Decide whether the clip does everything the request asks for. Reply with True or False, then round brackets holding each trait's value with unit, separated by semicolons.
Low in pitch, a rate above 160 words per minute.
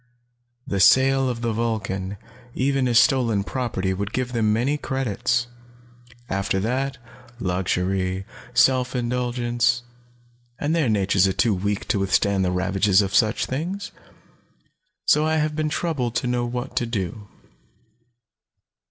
False (120 Hz; 135 wpm)